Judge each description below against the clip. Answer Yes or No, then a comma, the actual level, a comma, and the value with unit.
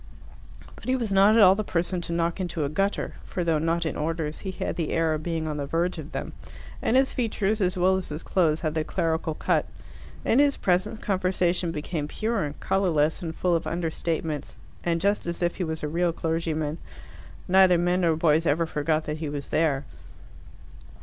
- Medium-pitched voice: Yes, medium, 170 Hz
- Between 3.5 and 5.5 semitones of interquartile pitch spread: No, average, 2.9 semitones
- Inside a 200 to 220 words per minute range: Yes, fast, 205 wpm